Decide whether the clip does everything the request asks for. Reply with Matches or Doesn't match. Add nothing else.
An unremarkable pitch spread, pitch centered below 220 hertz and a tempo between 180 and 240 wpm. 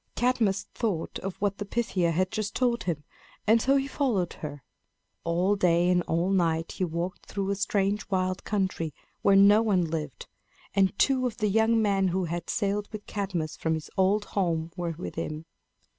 Matches